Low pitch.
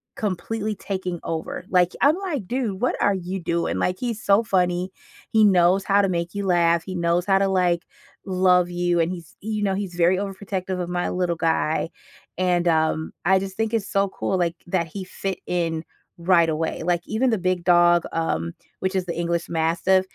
No: medium, 180 Hz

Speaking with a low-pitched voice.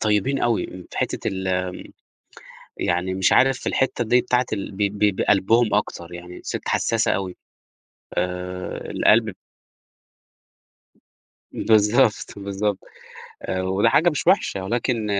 Yes: low, 105 Hz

